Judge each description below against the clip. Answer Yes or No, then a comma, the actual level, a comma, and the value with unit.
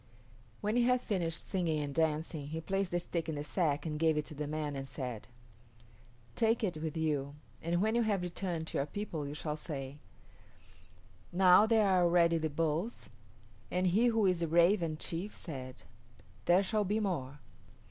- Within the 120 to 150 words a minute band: No, average, 185 wpm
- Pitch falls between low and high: Yes, medium, 165 Hz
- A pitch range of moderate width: Yes, average, 4.2 semitones